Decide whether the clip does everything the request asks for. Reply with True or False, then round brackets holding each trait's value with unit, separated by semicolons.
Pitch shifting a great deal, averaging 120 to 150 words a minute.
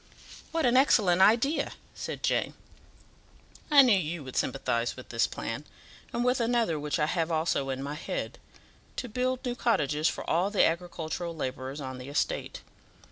False (9.0 semitones; 165 wpm)